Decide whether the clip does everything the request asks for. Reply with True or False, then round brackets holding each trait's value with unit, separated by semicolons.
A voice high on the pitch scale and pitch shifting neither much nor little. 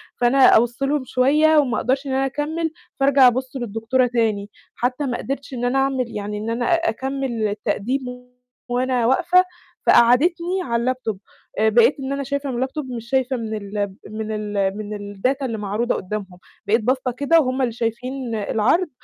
True (250 Hz; 3.6 semitones)